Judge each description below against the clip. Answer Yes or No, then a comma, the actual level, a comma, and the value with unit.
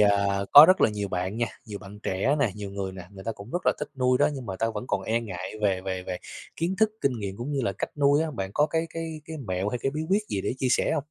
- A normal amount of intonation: No, wide, 6.7 semitones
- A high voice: No, low, 110 Hz